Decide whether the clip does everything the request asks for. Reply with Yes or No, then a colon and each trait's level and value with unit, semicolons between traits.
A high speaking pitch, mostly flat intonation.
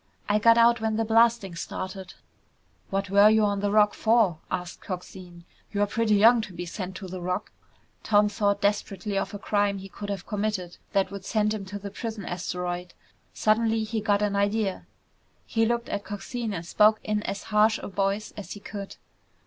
Yes: high, 205 Hz; narrow, 2.1 semitones